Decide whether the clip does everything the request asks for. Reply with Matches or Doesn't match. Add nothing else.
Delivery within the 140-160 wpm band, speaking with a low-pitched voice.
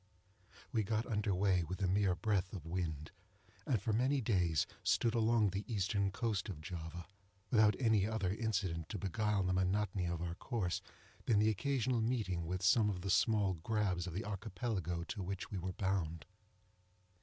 Doesn't match